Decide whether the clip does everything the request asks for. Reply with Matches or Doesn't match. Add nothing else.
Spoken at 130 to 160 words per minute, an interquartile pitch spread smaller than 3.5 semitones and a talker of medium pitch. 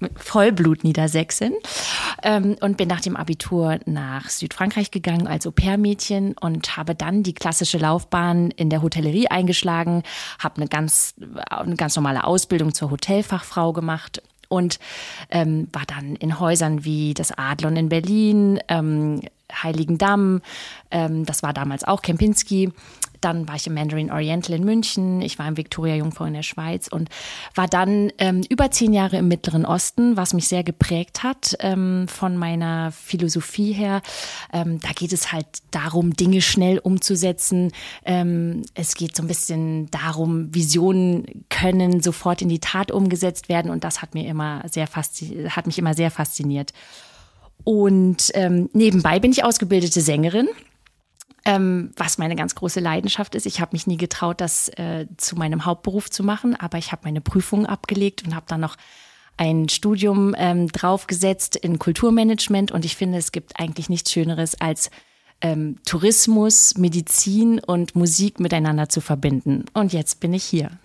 Matches